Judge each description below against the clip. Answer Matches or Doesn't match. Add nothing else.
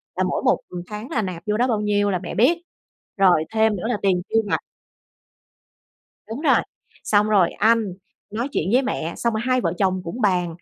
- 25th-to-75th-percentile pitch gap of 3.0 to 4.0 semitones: Matches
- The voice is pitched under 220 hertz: Matches